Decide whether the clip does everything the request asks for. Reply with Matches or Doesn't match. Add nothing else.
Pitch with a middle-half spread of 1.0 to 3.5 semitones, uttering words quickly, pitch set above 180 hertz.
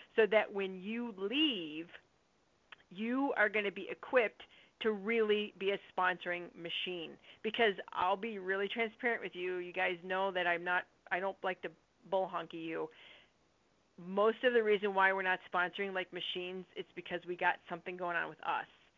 Doesn't match